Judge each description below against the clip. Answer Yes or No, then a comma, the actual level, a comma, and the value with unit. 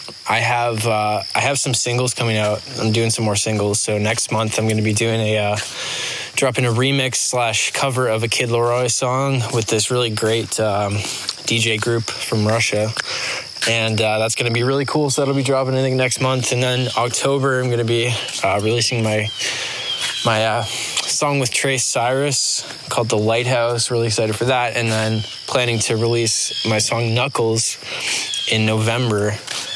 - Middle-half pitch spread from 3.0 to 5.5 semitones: No, narrow, 2.4 semitones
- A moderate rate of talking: Yes, average, 185 wpm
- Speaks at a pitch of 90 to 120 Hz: Yes, low, 115 Hz